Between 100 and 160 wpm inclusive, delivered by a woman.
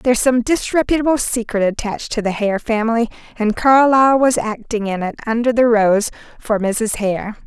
No: average, 170 wpm; female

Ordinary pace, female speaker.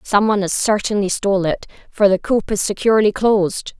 Yes: average, 175 wpm; female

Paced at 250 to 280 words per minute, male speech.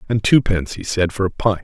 Yes: fast, 255 wpm; male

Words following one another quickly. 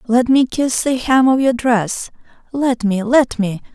No: average, 190 wpm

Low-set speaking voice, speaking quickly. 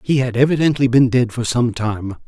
Yes: low, 125 Hz; fast, 210 wpm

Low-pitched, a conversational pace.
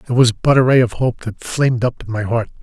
No: low, 120 Hz; fast, 300 wpm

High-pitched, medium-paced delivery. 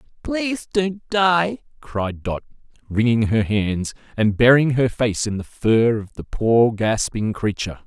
No: low, 125 Hz; average, 160 wpm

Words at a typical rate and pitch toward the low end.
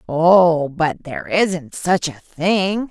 No: average, 145 wpm; medium, 170 Hz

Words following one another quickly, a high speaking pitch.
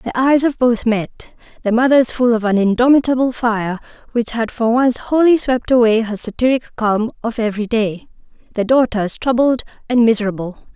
No: average, 160 wpm; high, 235 Hz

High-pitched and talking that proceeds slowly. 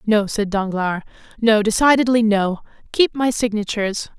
Yes: high, 215 Hz; slow, 130 wpm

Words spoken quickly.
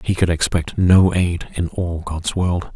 No: average, 195 wpm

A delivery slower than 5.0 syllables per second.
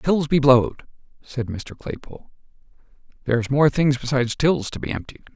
No: 5.3 syllables/s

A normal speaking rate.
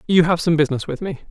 No: fast, 275 wpm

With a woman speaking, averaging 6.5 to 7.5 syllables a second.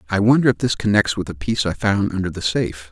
No: male; 6.7 syllables/s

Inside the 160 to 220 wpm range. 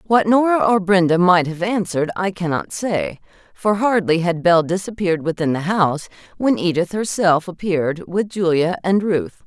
Yes: average, 165 wpm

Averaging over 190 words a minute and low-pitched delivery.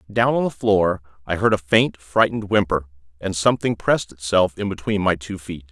Yes: average, 200 wpm; very low, 95 Hz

